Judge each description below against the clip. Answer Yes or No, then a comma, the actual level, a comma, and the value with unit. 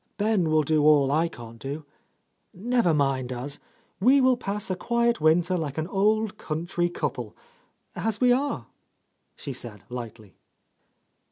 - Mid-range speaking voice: Yes, medium, 165 Hz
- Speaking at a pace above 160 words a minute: No, average, 155 wpm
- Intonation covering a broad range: Yes, wide, 7.4 semitones